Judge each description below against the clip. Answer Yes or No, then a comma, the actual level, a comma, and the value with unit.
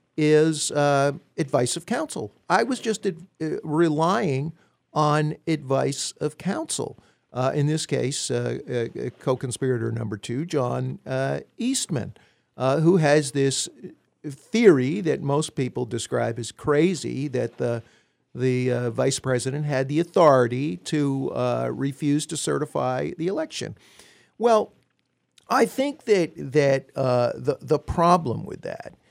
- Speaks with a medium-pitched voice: Yes, medium, 145 Hz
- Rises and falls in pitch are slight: No, average, 4.1 semitones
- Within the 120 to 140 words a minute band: Yes, slow, 135 wpm